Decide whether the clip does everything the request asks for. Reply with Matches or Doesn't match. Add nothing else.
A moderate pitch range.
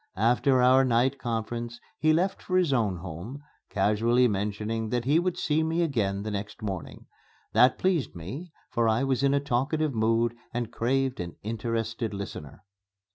Matches